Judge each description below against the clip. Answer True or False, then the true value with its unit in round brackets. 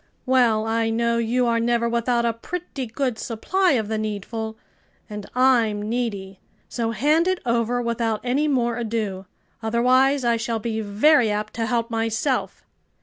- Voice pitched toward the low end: False (235 Hz)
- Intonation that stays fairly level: True (2.0 semitones)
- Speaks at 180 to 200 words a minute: False (155 wpm)